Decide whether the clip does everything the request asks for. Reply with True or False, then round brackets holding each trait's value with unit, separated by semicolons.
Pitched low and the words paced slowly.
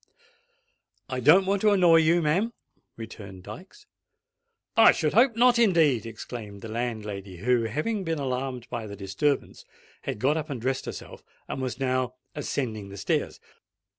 False (130 Hz; 155 wpm)